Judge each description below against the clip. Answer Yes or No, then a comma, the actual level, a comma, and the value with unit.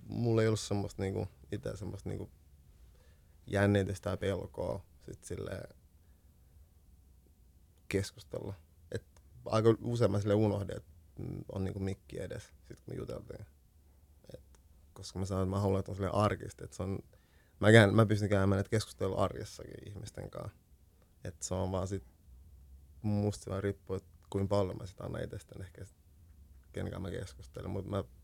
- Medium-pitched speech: No, very low, 95 Hz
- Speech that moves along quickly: No, average, 145 wpm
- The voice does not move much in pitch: No, average, 3.8 semitones